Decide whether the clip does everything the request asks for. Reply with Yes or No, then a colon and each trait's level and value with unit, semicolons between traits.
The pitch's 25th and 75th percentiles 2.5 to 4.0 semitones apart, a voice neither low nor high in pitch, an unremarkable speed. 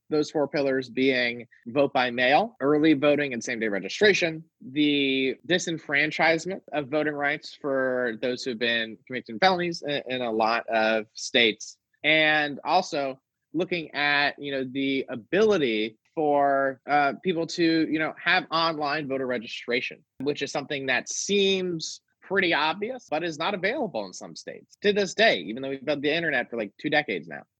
Yes: average, 3.7 semitones; medium, 145 Hz; average, 165 wpm